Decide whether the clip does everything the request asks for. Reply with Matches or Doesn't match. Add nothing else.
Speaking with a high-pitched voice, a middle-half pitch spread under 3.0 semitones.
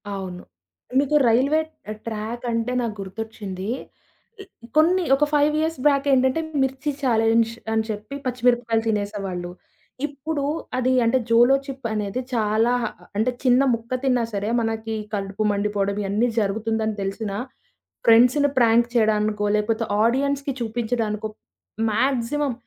Doesn't match